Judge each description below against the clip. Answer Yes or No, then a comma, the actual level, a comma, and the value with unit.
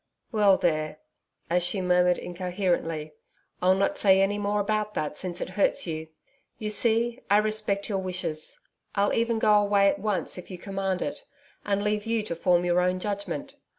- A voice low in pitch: No, high, 195 Hz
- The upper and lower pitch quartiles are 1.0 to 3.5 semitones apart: Yes, average, 2.7 semitones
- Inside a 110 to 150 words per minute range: No, average, 180 wpm